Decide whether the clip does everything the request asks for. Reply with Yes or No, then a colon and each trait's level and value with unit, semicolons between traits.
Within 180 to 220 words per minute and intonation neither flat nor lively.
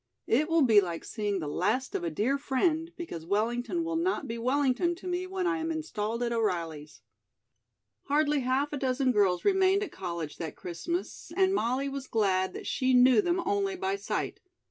No: average, 190 wpm; wide, 8.3 semitones